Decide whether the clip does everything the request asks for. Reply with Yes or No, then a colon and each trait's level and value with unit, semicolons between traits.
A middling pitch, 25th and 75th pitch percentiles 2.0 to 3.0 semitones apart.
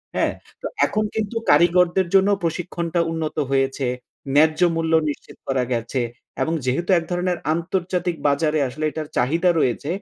No: medium, 165 Hz; average, 3.4 semitones